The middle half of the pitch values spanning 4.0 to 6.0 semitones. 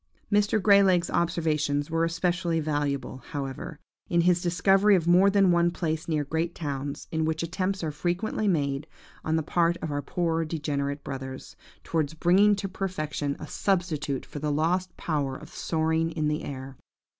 No: average, 3.3 semitones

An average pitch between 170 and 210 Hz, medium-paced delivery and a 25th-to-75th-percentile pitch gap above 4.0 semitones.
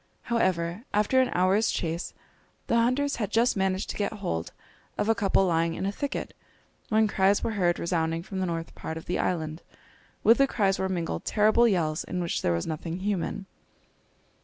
Yes: high, 190 Hz; average, 185 wpm; average, 4.4 semitones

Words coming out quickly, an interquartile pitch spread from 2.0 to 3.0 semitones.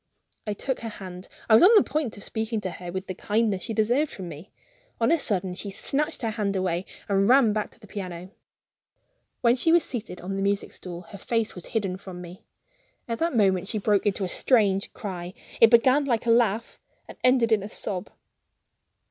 No: fast, 215 wpm; average, 3.7 semitones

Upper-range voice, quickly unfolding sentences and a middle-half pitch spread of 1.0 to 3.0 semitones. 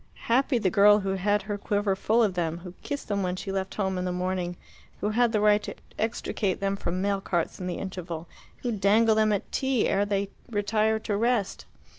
Yes: high, 200 Hz; fast, 215 wpm; narrow, 2.4 semitones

